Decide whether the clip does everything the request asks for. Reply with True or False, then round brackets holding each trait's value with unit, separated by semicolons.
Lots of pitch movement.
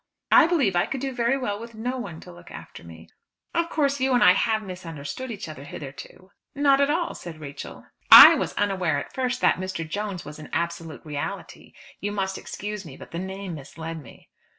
True (7.6 semitones)